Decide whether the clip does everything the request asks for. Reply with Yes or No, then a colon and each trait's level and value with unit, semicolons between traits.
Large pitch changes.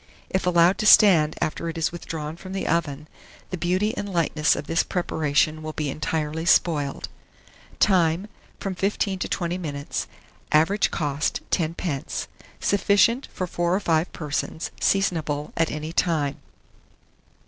No: average, 3.4 semitones